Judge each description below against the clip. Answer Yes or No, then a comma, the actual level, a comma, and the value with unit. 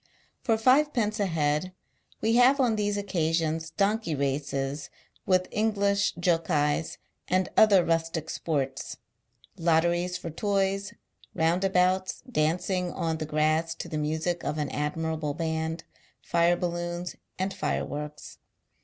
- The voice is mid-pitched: Yes, medium, 170 Hz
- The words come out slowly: Yes, slow, 125 wpm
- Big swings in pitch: No, average, 3.8 semitones